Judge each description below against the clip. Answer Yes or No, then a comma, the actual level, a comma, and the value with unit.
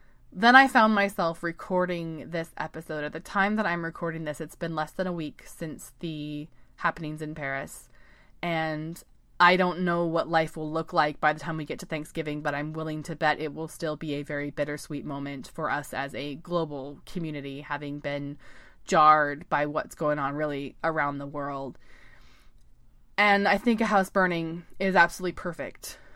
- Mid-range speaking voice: Yes, medium, 155 Hz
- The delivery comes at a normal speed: Yes, average, 185 wpm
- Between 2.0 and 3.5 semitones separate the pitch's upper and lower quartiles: Yes, average, 2.7 semitones